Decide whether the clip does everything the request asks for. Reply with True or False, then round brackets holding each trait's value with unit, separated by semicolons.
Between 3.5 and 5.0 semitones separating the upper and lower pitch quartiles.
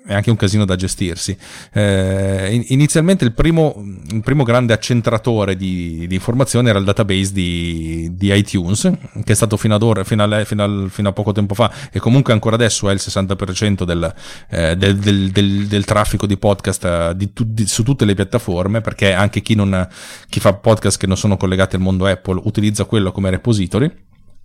False (2.8 semitones)